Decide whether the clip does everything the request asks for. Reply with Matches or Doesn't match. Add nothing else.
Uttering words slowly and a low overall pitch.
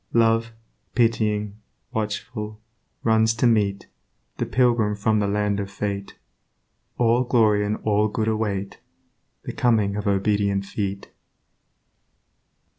Matches